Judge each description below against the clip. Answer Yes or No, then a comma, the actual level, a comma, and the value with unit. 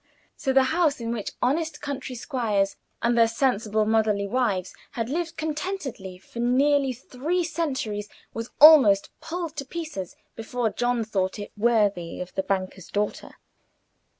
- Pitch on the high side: Yes, high, 240 Hz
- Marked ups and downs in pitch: Yes, wide, 5.7 semitones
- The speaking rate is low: No, average, 145 wpm